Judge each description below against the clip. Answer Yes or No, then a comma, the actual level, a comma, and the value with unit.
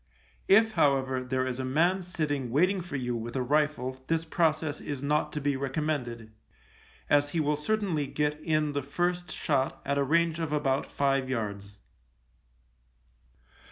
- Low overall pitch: No, medium, 145 Hz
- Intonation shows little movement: No, average, 3.3 semitones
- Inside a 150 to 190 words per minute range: Yes, average, 160 wpm